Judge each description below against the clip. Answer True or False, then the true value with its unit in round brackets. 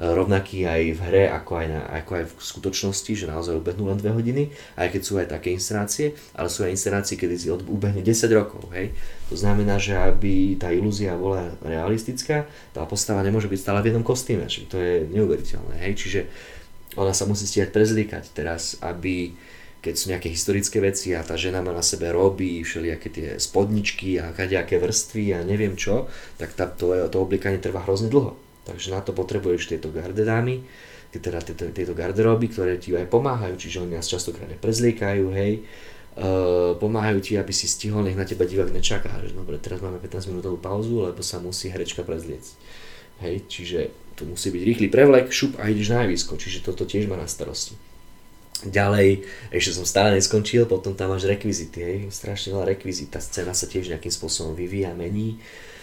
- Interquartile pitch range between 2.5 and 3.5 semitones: True (2.9 semitones)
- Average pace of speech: False (185 wpm)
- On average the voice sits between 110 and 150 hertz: False (95 Hz)